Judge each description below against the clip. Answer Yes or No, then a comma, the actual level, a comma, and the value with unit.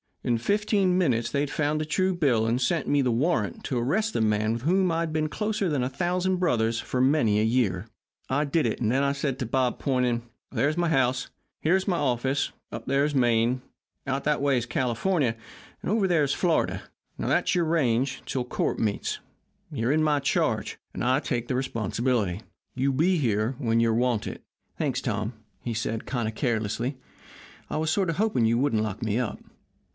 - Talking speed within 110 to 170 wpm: No, fast, 205 wpm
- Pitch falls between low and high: No, low, 130 Hz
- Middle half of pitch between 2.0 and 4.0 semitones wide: No, average, 5.0 semitones